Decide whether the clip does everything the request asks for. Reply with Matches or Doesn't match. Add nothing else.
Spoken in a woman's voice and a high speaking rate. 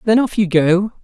Doesn't match